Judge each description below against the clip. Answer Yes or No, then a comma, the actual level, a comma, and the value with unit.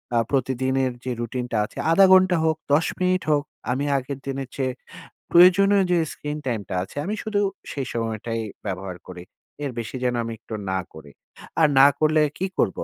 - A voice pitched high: No, low, 135 Hz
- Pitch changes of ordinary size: No, wide, 5.7 semitones